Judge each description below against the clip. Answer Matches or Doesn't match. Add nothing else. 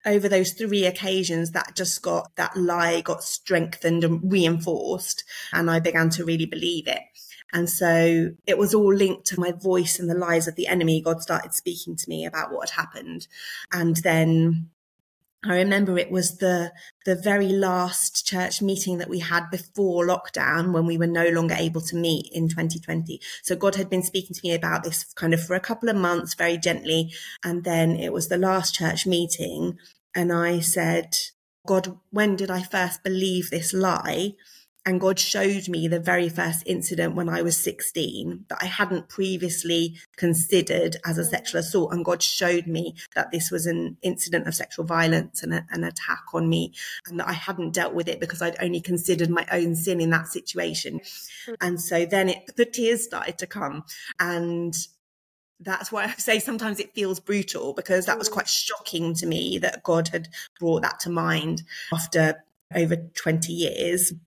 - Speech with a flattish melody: Matches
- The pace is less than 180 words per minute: Doesn't match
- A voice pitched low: Doesn't match